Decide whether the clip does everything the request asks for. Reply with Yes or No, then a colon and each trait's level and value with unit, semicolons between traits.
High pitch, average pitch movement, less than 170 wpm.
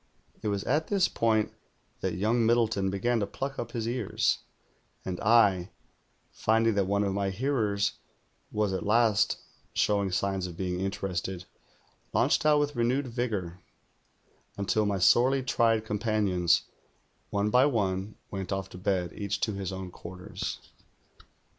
No: low, 105 Hz; average, 3.4 semitones; average, 145 wpm